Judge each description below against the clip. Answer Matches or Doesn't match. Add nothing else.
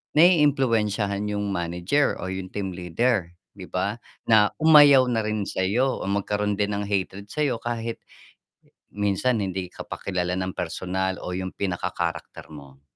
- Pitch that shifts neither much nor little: Matches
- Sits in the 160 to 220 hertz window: Doesn't match